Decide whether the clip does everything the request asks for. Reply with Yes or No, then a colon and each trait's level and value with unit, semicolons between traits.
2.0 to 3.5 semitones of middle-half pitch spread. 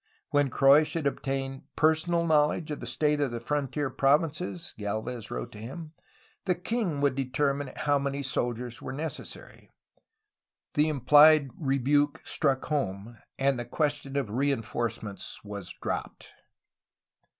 Yes: average, 3.0 semitones